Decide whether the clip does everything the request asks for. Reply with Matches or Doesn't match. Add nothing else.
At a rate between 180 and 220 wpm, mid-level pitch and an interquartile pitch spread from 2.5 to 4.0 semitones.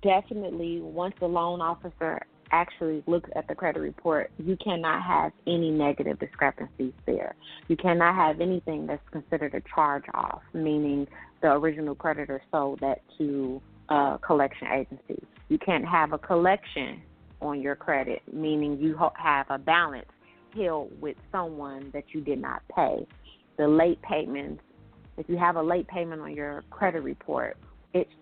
Doesn't match